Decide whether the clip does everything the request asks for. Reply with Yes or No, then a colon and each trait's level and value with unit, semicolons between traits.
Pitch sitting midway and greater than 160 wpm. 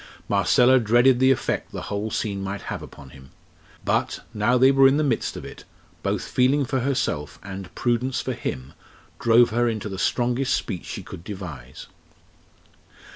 No: low, 120 Hz; average, 170 wpm